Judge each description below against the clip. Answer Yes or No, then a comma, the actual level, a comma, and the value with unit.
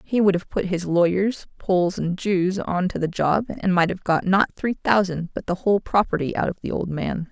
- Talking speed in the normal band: No, fast, 240 wpm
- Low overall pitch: No, medium, 185 Hz